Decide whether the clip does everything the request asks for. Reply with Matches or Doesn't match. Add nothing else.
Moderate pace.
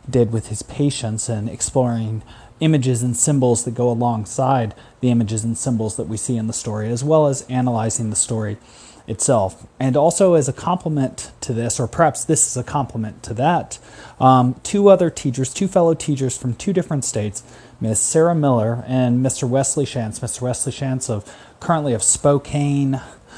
Matches